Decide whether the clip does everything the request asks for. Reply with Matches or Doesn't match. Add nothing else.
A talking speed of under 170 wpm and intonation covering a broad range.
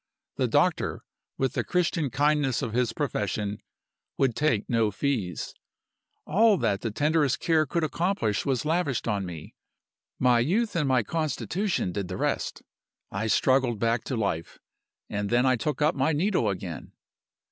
Matches